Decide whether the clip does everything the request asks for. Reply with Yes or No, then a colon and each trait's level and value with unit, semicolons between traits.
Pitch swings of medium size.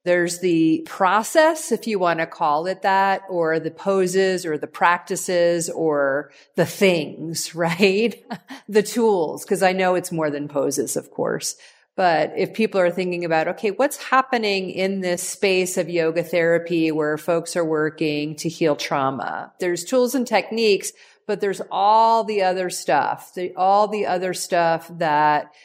Yes: average, 3.5 semitones